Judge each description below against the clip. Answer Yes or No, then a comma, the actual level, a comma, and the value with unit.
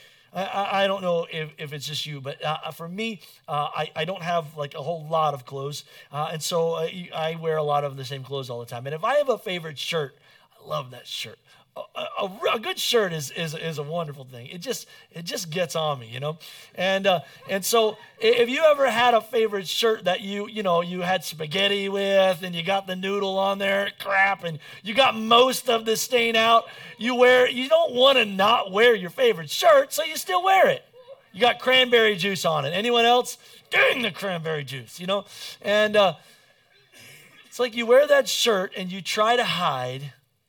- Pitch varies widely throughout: Yes, wide, 6.4 semitones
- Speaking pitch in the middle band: No, high, 195 Hz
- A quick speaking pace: Yes, fast, 220 wpm